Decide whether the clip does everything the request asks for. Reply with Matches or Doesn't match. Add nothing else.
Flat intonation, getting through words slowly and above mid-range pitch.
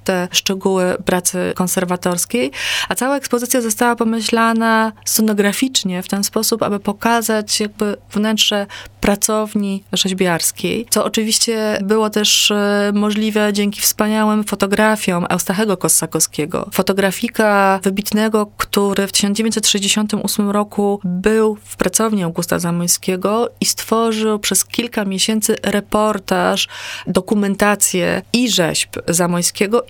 Matches